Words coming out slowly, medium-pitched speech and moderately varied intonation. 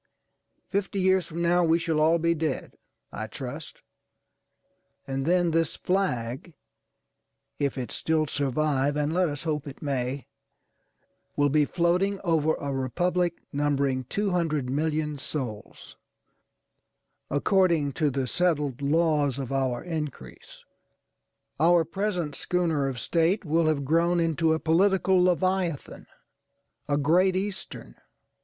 Yes: slow, 120 wpm; medium, 155 Hz; average, 3.7 semitones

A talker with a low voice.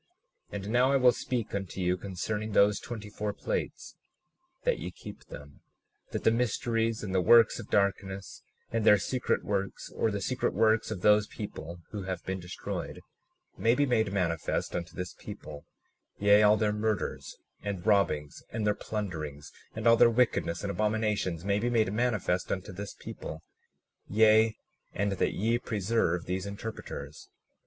Yes: low, 105 Hz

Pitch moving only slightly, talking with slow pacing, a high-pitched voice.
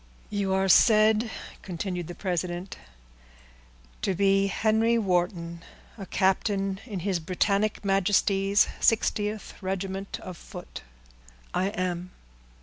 Yes: narrow, 2.1 semitones; slow, 105 wpm; high, 195 Hz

